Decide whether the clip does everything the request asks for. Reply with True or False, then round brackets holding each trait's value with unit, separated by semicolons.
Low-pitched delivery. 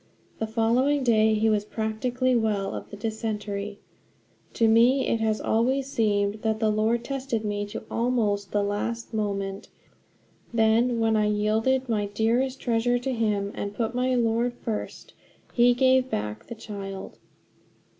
False (225 Hz)